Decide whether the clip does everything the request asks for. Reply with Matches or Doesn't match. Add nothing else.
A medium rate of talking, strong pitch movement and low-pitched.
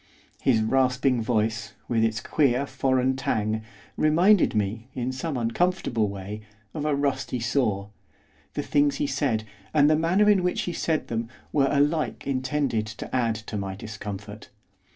Doesn't match